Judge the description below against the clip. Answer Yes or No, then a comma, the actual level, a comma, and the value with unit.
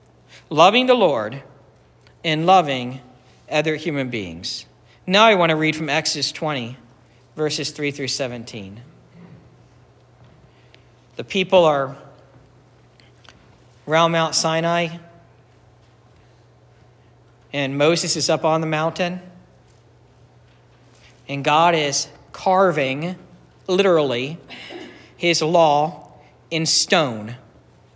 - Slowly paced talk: Yes, slow, 90 wpm